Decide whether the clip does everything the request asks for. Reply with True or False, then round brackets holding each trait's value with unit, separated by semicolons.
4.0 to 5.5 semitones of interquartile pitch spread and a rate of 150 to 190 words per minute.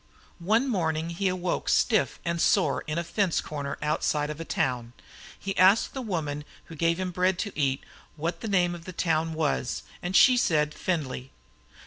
False (3.5 semitones; 180 wpm)